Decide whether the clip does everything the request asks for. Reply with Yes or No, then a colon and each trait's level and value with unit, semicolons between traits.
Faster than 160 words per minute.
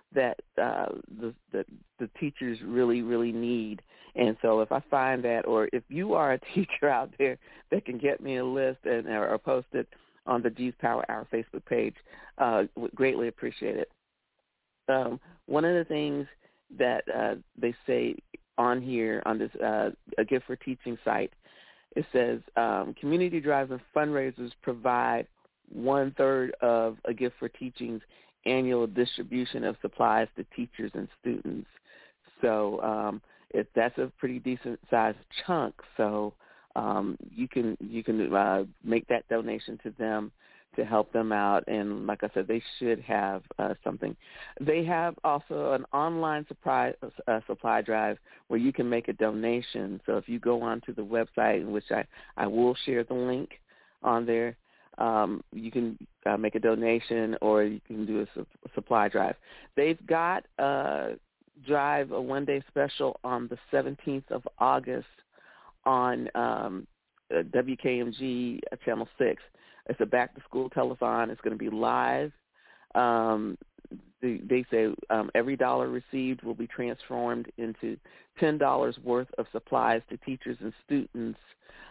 No: average, 155 wpm